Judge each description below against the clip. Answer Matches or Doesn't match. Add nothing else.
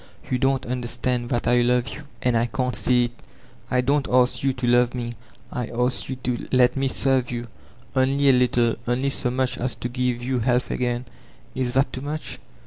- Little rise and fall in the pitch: Matches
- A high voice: Doesn't match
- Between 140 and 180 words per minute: Doesn't match